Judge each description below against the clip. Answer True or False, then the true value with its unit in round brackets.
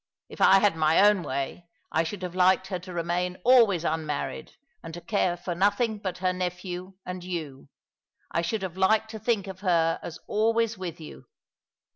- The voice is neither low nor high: True (180 Hz)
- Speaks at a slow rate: False (185 wpm)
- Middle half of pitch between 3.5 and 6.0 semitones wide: False (3.0 semitones)